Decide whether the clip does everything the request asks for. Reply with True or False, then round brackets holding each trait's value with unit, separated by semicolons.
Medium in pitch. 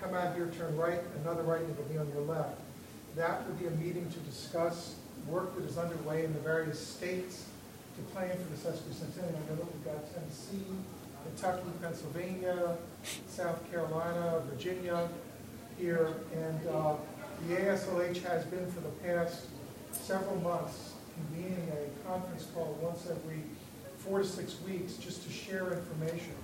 True (170 Hz)